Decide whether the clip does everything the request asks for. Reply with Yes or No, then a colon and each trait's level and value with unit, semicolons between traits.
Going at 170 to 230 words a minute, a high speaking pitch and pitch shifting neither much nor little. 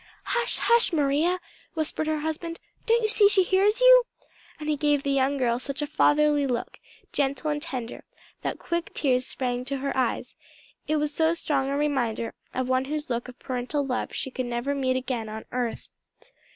Yes: average, 190 wpm; very high, 285 Hz; average, 3.5 semitones